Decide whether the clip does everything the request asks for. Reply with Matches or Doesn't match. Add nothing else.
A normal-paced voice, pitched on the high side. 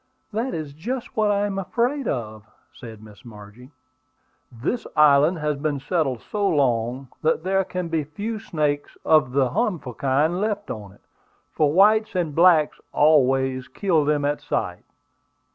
Doesn't match